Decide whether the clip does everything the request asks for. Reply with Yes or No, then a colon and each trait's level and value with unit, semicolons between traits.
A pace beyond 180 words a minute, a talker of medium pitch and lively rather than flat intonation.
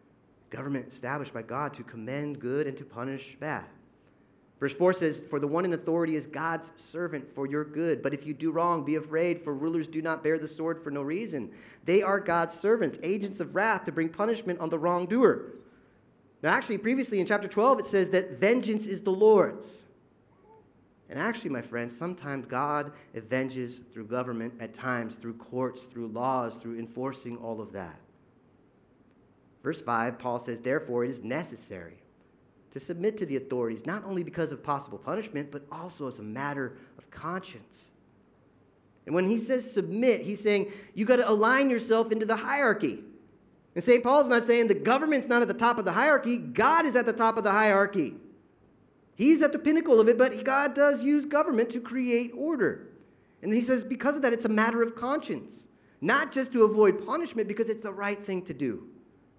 Yes: average, 190 wpm; medium, 175 Hz; wide, 8.6 semitones